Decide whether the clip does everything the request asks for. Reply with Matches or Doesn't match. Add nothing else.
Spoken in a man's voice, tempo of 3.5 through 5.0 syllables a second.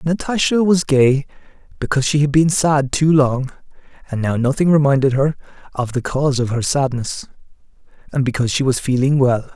Doesn't match